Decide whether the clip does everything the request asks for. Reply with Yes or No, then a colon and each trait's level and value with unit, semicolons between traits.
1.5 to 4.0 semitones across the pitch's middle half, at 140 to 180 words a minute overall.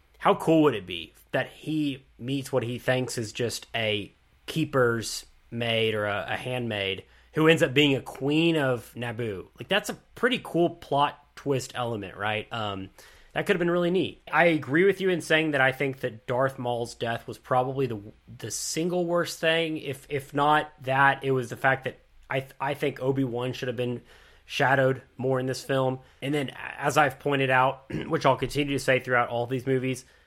No: average, 3.5 semitones; average, 200 wpm